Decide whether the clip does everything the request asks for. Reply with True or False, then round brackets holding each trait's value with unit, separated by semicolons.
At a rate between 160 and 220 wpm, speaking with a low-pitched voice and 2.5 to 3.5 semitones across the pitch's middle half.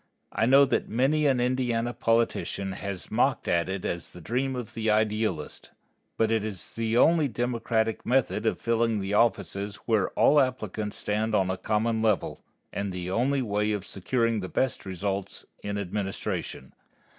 True (165 wpm; 110 Hz; 3.2 semitones)